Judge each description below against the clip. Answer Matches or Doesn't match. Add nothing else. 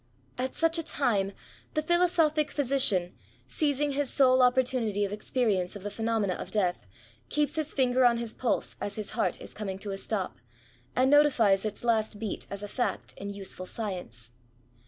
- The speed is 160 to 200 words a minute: Matches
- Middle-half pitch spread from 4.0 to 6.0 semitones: Matches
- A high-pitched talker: Matches